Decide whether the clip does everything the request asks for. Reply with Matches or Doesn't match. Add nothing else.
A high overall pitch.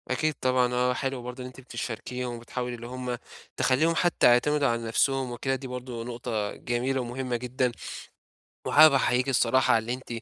Doesn't match